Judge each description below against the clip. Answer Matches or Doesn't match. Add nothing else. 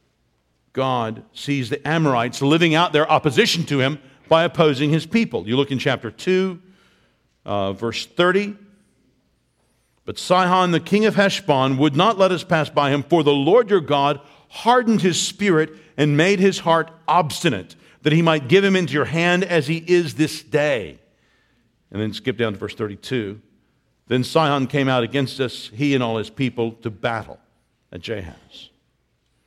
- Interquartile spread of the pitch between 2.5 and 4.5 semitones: Doesn't match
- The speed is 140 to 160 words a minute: Doesn't match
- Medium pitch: Matches